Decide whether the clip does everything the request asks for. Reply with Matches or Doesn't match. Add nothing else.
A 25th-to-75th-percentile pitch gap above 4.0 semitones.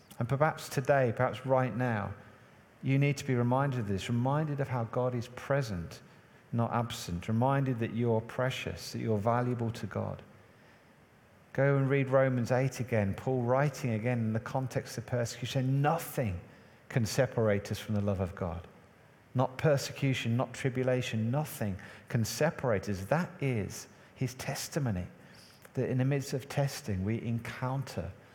Doesn't match